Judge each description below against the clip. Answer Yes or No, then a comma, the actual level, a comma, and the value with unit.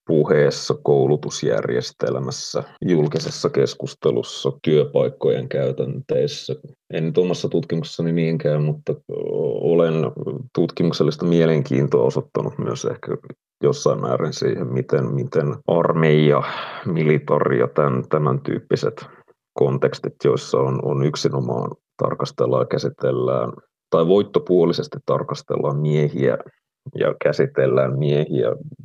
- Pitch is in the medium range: No, very low, 75 Hz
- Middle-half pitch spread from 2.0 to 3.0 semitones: Yes, narrow, 2.4 semitones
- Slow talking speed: Yes, slow, 90 wpm